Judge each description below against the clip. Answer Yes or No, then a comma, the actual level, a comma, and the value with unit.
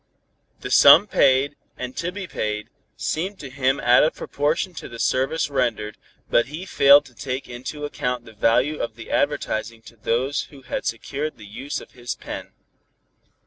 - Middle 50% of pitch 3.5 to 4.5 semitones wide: Yes, average, 3.9 semitones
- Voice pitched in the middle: No, low, 130 Hz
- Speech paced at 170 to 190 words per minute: Yes, average, 175 wpm